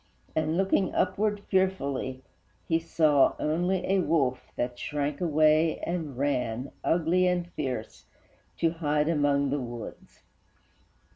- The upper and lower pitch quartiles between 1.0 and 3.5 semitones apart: No, average, 4.0 semitones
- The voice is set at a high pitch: No, medium, 155 Hz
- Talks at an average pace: No, slow, 120 wpm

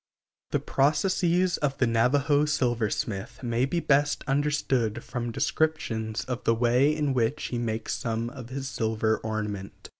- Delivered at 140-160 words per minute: Yes, average, 145 wpm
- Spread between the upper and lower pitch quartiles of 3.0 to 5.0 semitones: Yes, average, 4.2 semitones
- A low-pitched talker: Yes, low, 125 Hz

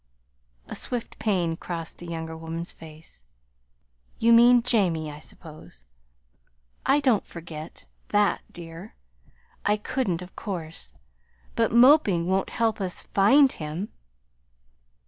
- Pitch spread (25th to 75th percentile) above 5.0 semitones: Yes, wide, 5.5 semitones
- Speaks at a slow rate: Yes, slow, 115 wpm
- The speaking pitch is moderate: Yes, medium, 180 Hz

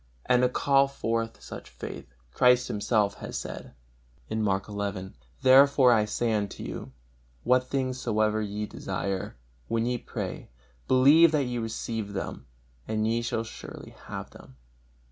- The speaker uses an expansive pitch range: No, average, 3.2 semitones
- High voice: No, low, 115 Hz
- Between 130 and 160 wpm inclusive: Yes, average, 145 wpm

